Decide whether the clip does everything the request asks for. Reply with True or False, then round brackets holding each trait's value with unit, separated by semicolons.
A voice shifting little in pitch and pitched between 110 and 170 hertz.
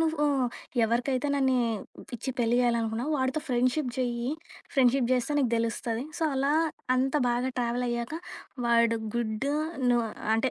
False (2.0 semitones; 245 Hz)